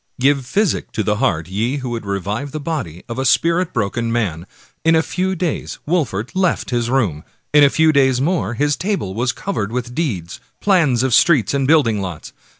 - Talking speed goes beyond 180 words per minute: Yes, average, 195 wpm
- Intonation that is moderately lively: No, wide, 6.7 semitones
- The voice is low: Yes, low, 130 Hz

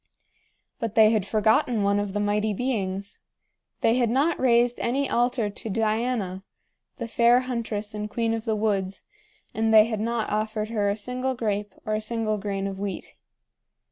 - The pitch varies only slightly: Yes, narrow, 2.2 semitones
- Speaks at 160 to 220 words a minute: Yes, average, 170 wpm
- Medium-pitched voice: No, high, 220 Hz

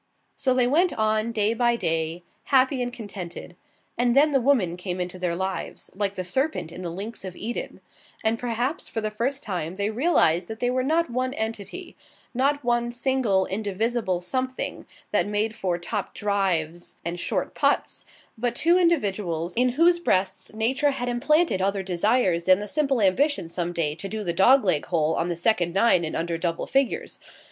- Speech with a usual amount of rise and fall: No, wide, 6.0 semitones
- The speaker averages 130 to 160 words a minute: No, average, 185 wpm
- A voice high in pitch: Yes, high, 215 Hz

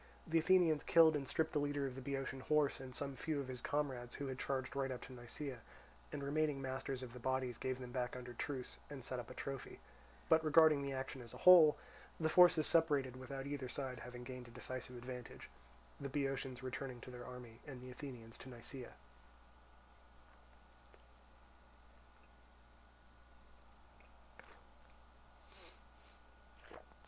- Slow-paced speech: No, average, 155 wpm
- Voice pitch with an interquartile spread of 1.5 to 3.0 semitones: Yes, narrow, 2.4 semitones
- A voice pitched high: No, low, 135 Hz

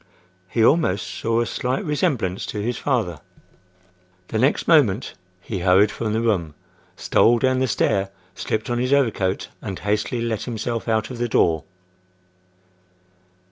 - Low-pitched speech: Yes, low, 115 Hz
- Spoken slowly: No, average, 145 wpm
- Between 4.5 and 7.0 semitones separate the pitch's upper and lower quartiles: No, average, 3.9 semitones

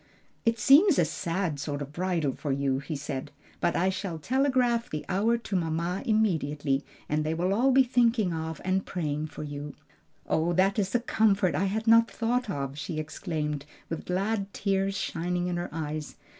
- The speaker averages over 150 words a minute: Yes, average, 185 wpm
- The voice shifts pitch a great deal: Yes, wide, 6.0 semitones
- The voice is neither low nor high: Yes, medium, 180 Hz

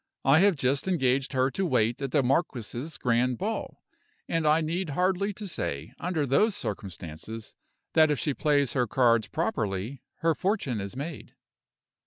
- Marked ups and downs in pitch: Yes, wide, 5.7 semitones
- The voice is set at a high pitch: No, low, 135 Hz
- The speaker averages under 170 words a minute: Yes, average, 155 wpm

